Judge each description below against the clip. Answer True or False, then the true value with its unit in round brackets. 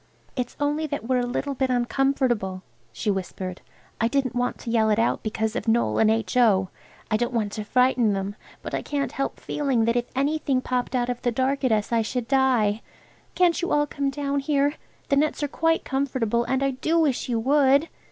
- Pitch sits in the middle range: False (250 Hz)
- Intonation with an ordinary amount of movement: True (3.7 semitones)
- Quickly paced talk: True (210 wpm)